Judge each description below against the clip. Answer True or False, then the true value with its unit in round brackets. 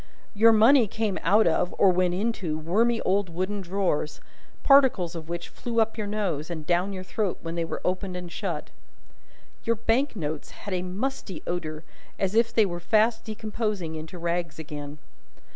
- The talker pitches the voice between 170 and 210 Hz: True (185 Hz)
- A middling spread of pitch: True (4.4 semitones)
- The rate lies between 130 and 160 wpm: False (175 wpm)